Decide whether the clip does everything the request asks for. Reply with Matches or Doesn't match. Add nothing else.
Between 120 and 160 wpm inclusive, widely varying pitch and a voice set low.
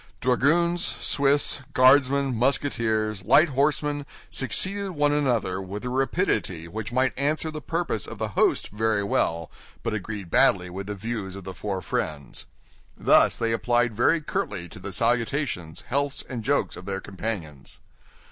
Matches